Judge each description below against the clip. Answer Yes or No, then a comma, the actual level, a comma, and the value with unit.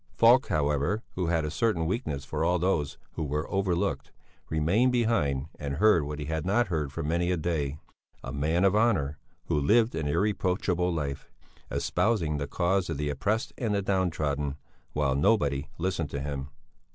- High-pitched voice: No, very low, 80 Hz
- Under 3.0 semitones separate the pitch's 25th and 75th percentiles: No, average, 5.0 semitones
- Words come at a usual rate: Yes, average, 175 wpm